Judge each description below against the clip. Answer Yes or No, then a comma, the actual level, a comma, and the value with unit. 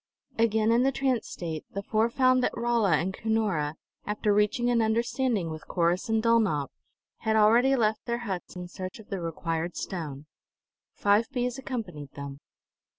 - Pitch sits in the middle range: No, high, 215 Hz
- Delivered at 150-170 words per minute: Yes, average, 160 wpm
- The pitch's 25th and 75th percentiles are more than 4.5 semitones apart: Yes, average, 5.2 semitones